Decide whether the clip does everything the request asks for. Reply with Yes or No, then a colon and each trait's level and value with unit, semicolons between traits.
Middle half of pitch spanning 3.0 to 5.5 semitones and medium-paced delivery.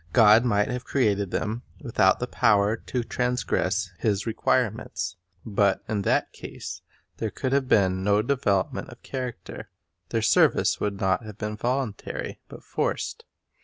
Yes: average, 3.5 semitones; average, 150 wpm